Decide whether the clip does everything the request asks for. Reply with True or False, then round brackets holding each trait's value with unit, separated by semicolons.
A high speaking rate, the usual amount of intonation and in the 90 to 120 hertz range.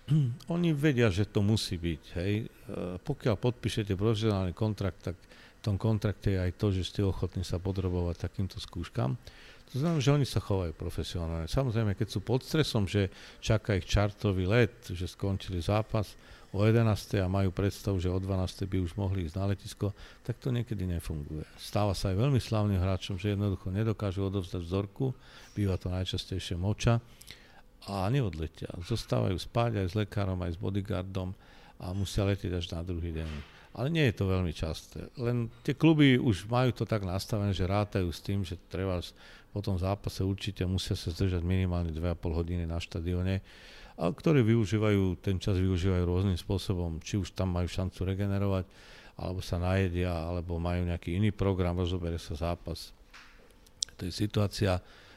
True (170 wpm; 3.0 semitones; 100 Hz)